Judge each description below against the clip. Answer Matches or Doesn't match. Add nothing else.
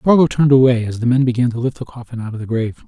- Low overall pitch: Matches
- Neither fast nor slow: Doesn't match